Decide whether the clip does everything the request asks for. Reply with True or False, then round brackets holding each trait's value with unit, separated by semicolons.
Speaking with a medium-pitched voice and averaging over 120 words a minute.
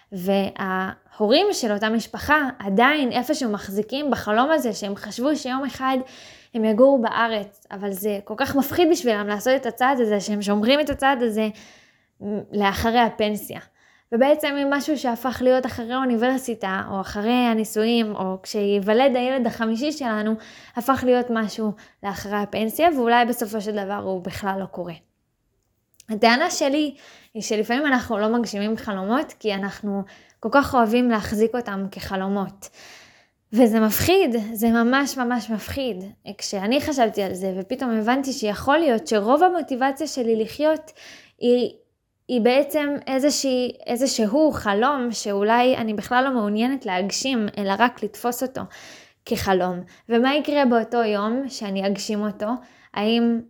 False (230 Hz; 135 wpm)